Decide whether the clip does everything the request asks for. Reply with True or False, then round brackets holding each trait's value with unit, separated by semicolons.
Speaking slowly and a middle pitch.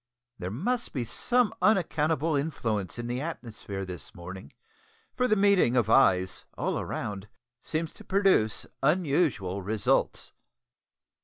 False (125 wpm; 130 Hz)